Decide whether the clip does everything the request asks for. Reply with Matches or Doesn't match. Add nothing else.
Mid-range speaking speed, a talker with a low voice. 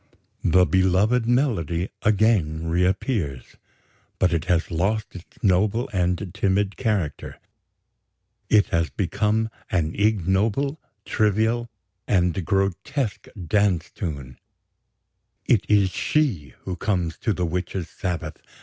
Doesn't match